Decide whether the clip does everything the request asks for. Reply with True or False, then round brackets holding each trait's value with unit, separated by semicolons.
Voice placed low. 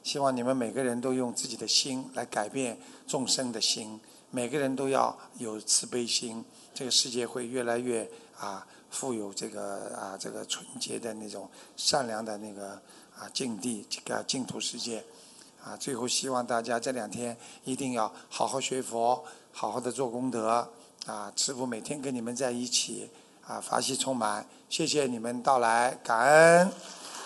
True (125 Hz)